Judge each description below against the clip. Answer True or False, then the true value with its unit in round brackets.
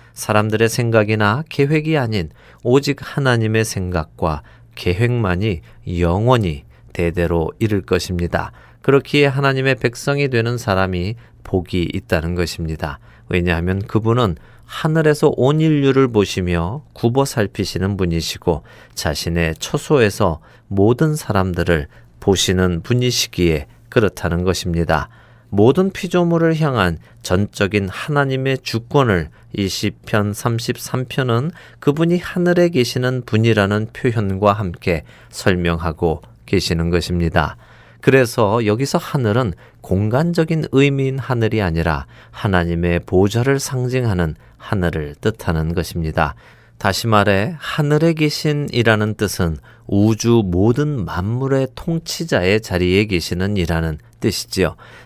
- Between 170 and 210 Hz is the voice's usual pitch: False (110 Hz)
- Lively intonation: True (6.1 semitones)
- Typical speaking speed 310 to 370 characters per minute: False (275 characters per minute)